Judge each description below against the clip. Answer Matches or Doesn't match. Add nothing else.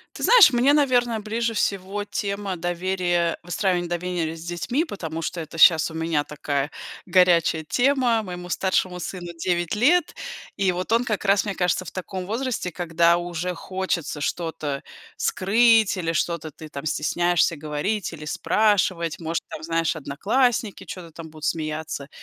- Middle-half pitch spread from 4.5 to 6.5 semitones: Doesn't match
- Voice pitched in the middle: Matches